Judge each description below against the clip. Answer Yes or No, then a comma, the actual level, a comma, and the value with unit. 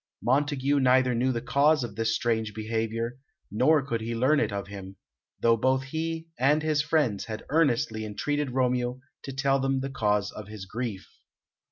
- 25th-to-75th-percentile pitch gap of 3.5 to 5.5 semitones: Yes, average, 3.8 semitones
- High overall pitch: No, low, 125 Hz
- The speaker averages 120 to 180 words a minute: Yes, average, 175 wpm